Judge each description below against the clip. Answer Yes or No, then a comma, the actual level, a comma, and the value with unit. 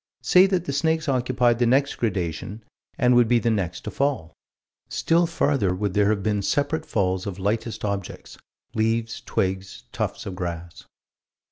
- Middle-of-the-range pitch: No, low, 110 Hz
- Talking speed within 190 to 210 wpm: No, average, 160 wpm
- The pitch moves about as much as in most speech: No, wide, 5.7 semitones